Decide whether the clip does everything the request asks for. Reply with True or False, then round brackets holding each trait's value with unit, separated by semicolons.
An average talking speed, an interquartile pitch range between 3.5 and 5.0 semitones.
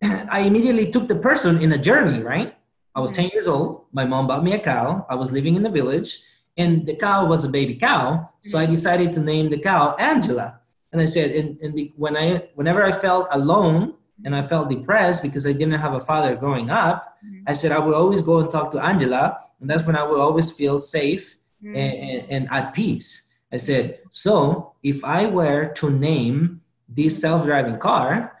False (210 wpm; 3.8 semitones)